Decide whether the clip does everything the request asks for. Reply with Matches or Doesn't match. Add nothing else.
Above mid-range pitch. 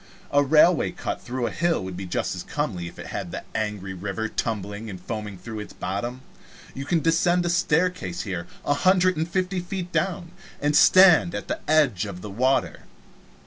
Doesn't match